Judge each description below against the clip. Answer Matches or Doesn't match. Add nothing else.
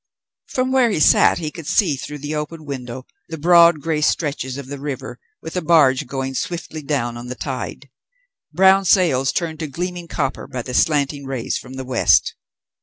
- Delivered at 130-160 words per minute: Doesn't match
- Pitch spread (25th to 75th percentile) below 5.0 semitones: Matches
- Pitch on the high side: Doesn't match